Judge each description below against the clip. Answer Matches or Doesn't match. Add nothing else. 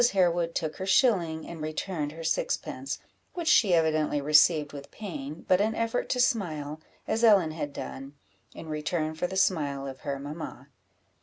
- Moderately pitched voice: Matches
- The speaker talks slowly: Doesn't match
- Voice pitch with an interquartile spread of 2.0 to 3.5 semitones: Doesn't match